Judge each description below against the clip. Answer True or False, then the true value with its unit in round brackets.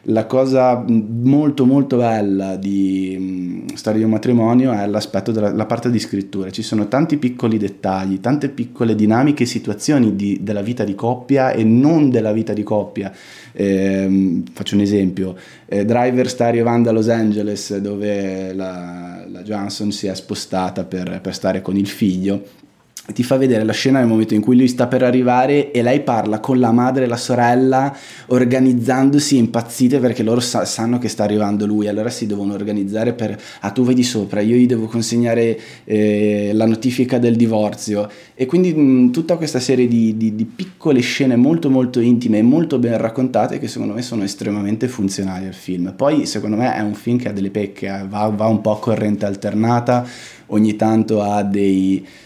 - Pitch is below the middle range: True (110 Hz)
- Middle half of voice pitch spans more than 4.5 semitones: False (3.4 semitones)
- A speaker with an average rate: False (185 wpm)